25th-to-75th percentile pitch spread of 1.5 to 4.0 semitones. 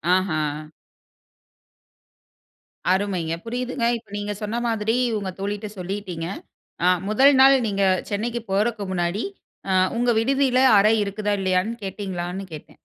Yes: average, 3.5 semitones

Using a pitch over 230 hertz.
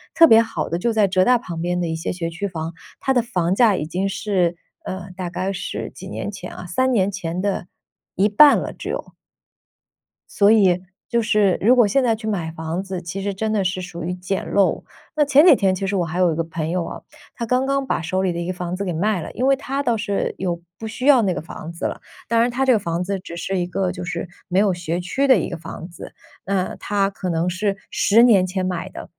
No: high, 190 Hz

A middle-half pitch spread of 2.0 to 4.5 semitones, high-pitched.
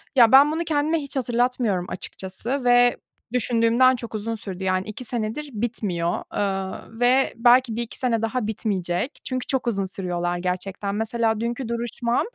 Yes: average, 4.0 semitones; high, 230 Hz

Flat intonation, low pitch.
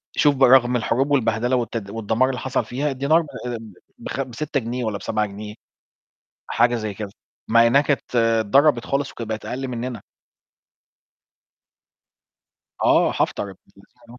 No: average, 3.1 semitones; low, 120 Hz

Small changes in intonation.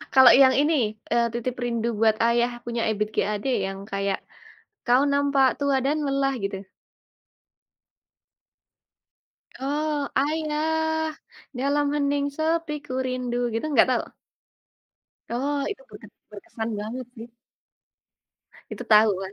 No: average, 3.8 semitones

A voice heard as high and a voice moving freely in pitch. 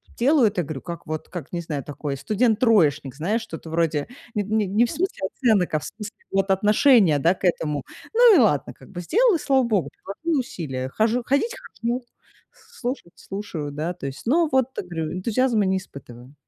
Yes: high, 195 Hz; wide, 7.4 semitones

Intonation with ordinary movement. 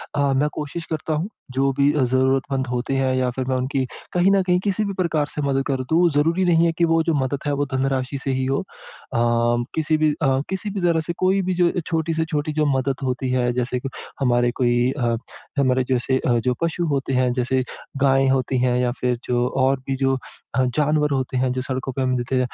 Yes: average, 3.5 semitones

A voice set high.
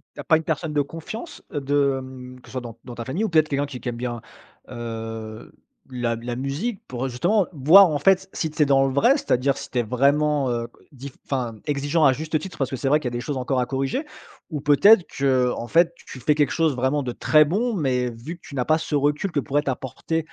No: medium, 140 Hz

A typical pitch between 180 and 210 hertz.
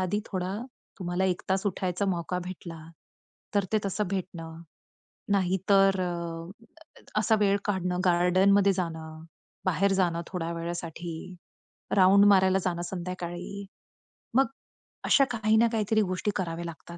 Yes: medium, 185 Hz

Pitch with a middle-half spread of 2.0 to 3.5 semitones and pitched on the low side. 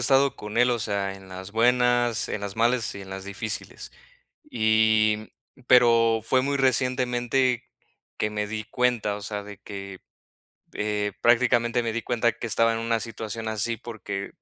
Yes: narrow, 2.6 semitones; low, 115 Hz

